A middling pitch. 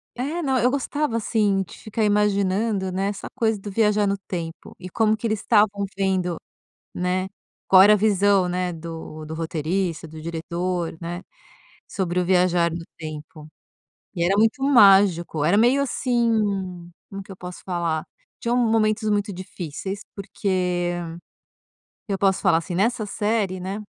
No: high, 195 Hz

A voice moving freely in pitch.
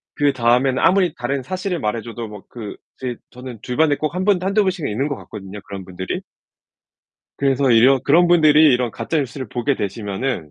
No: average, 5.0 semitones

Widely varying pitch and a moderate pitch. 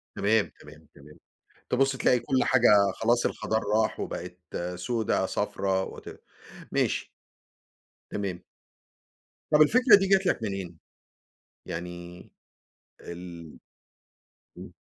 No: wide, 5.8 semitones; low, 100 Hz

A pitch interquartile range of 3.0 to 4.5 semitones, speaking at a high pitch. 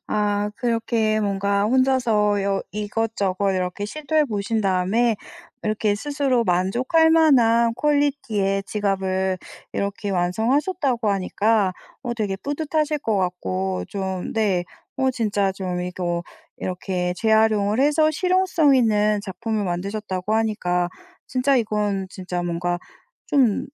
Yes: average, 4.1 semitones; high, 210 Hz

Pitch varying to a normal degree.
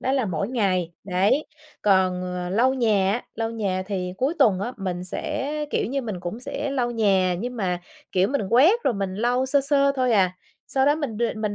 No: wide, 5.8 semitones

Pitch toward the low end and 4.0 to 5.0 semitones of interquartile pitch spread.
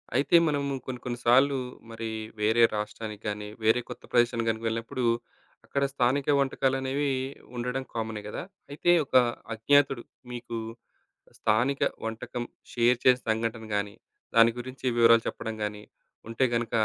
No: low, 120 Hz; average, 2.9 semitones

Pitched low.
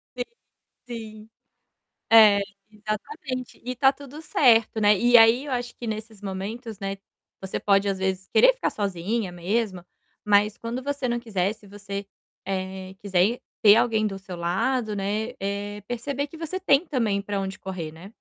No: high, 215 Hz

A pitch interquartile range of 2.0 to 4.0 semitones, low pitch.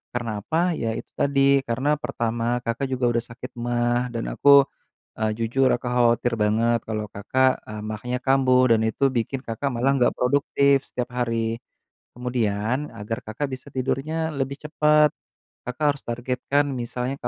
Yes: average, 2.9 semitones; low, 125 Hz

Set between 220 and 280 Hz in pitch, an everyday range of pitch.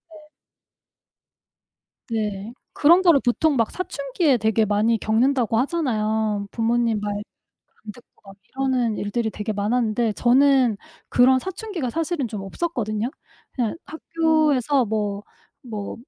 Yes: high, 240 Hz; average, 4.7 semitones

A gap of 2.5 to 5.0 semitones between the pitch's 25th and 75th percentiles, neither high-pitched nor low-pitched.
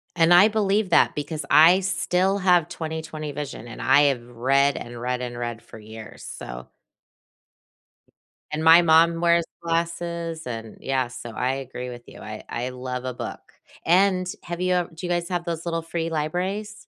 No: wide, 5.5 semitones; medium, 160 Hz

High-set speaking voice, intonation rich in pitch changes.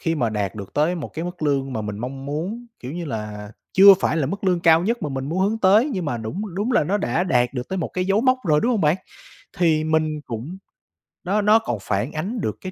No: medium, 160 Hz; wide, 6.4 semitones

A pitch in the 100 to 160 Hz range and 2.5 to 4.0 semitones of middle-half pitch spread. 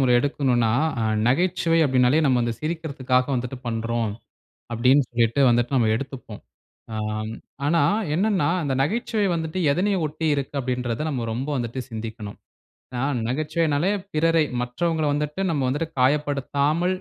No: medium, 140 Hz; average, 4.6 semitones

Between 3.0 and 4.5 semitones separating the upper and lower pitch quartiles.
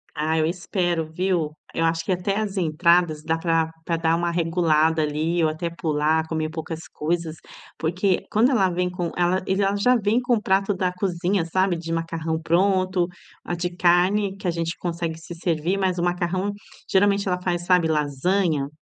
No: narrow, 2.5 semitones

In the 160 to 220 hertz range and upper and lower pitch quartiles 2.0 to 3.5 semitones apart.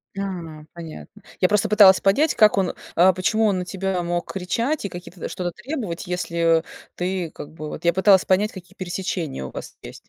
Yes: medium, 185 Hz; narrow, 2.5 semitones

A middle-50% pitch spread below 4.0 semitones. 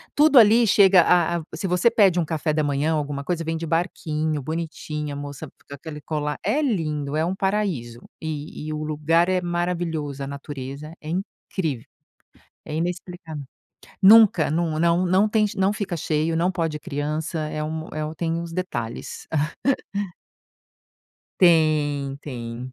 Yes: average, 3.1 semitones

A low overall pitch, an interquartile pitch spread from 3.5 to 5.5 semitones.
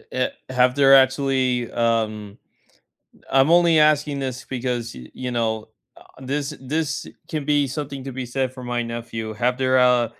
No: low, 130 Hz; narrow, 2.6 semitones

